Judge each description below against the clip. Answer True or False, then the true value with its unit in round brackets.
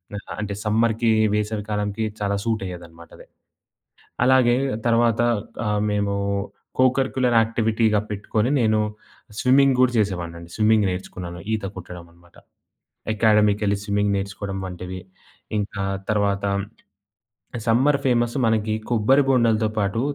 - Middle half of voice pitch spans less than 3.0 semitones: True (2.6 semitones)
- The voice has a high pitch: False (105 Hz)